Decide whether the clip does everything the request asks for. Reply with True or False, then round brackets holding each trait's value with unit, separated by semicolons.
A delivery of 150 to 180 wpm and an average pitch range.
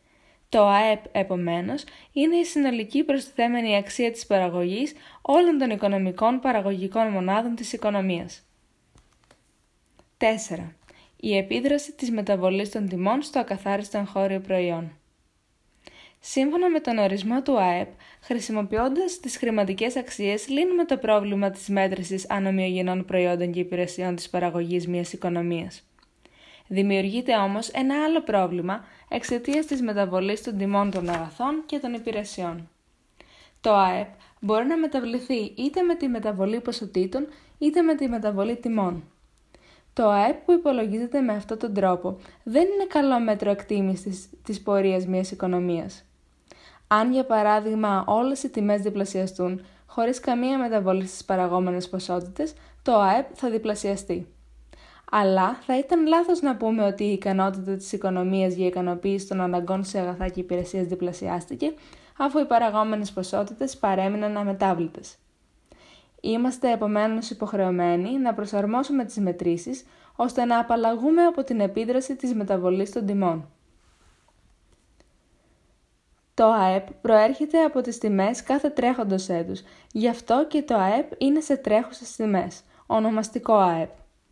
False (125 wpm; 4.8 semitones)